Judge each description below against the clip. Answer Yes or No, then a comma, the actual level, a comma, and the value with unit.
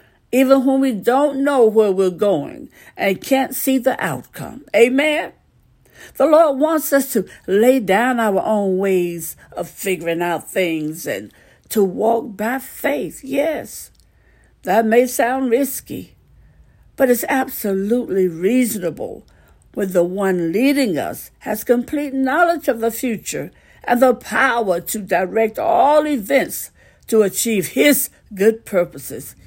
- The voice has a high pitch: Yes, high, 230 Hz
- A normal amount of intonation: No, wide, 5.7 semitones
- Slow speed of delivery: Yes, slow, 130 wpm